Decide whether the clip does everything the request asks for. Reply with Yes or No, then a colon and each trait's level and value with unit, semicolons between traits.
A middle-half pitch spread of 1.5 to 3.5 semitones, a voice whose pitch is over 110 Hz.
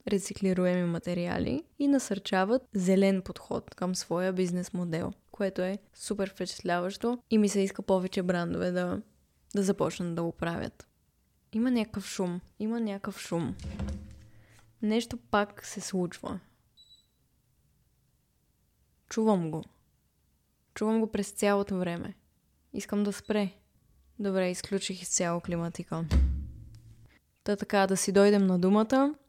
Yes: average, 2.8 semitones; high, 190 Hz